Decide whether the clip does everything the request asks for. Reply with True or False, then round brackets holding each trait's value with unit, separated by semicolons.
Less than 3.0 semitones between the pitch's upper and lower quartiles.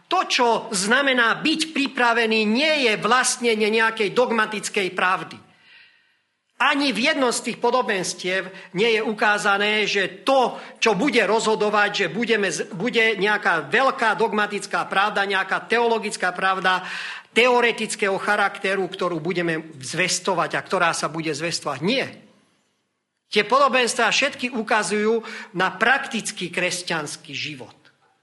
False (4.0 semitones)